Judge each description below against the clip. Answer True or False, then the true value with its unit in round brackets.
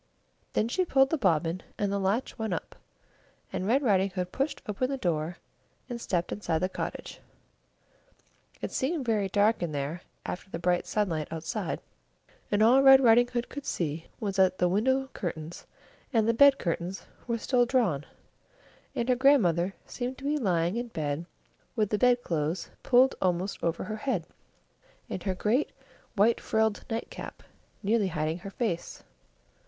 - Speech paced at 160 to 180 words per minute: True (165 wpm)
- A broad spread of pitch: True (5.8 semitones)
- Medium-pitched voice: False (205 Hz)